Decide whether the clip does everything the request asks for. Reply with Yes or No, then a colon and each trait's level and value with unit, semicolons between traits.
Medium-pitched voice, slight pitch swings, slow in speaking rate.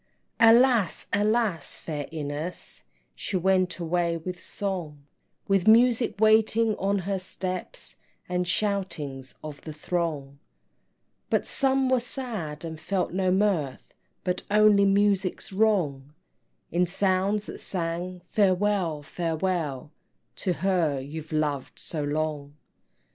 No: medium, 180 Hz; average, 4.5 semitones; slow, 115 wpm